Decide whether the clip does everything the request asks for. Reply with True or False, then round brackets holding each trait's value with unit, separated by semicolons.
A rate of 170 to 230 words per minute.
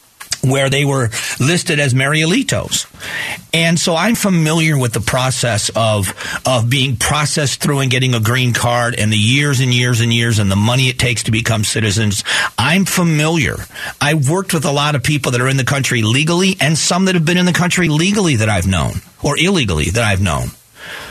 True (200 wpm)